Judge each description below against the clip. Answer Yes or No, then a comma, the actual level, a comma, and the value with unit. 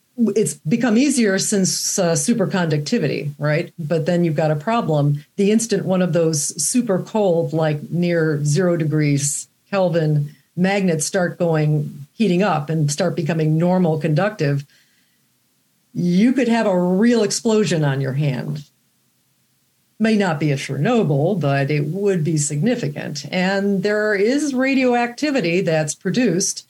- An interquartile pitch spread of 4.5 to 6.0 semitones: Yes, average, 4.9 semitones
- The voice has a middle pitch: Yes, medium, 175 Hz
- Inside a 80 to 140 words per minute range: Yes, slow, 135 wpm